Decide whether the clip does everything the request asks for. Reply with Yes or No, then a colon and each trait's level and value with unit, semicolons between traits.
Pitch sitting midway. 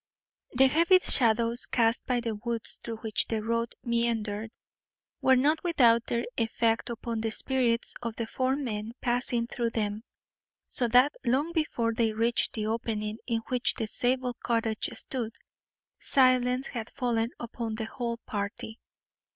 No: high, 235 Hz